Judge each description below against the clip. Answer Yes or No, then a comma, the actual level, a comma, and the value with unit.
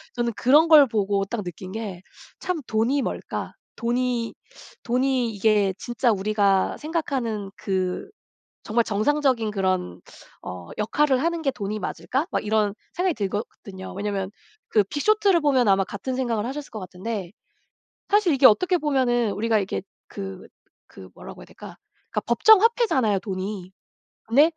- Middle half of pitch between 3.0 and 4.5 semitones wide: No, wide, 5.5 semitones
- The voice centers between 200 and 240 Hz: Yes, high, 225 Hz